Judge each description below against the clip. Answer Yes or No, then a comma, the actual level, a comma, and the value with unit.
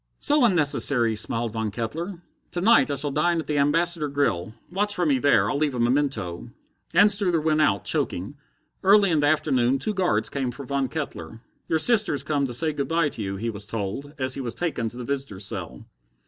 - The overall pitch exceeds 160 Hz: No, medium, 140 Hz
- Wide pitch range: Yes, wide, 5.8 semitones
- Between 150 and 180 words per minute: No, fast, 205 wpm